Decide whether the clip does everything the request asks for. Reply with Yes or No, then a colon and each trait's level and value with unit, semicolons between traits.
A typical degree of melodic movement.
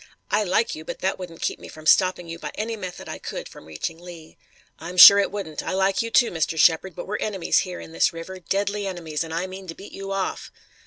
Yes: average, 3.0 semitones